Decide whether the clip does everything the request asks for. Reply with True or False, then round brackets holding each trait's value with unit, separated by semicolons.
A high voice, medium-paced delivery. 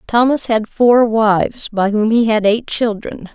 True (220 Hz; 180 wpm)